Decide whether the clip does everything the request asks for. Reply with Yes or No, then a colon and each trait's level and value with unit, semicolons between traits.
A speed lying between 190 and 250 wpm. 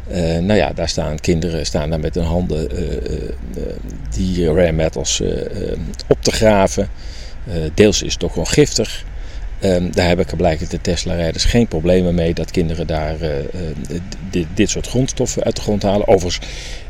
No: average, 180 wpm